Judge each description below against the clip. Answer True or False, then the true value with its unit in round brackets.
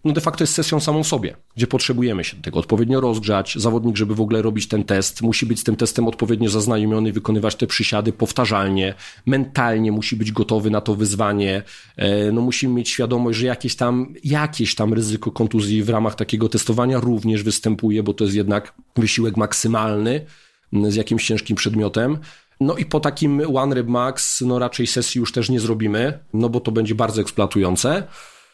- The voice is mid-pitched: False (115 Hz)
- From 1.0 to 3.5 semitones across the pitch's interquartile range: True (2.6 semitones)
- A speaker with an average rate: False (180 wpm)